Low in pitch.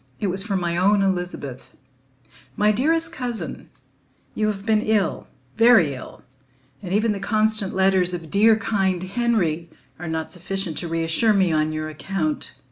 No: high, 195 Hz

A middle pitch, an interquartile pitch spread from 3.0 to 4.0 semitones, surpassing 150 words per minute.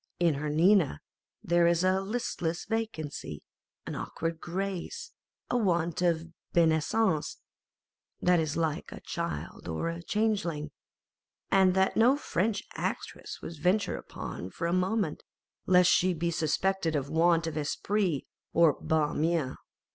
No: medium, 170 Hz; average, 3.3 semitones; average, 145 wpm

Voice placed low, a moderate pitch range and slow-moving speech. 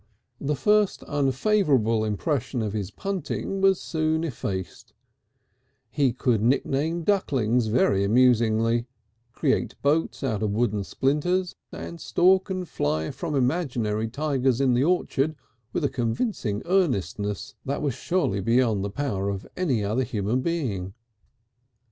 No: low, 130 Hz; wide, 6.5 semitones; slow, 130 wpm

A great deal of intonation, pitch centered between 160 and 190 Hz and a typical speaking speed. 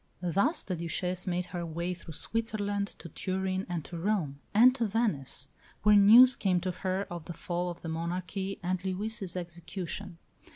No: average, 2.9 semitones; medium, 185 Hz; average, 170 wpm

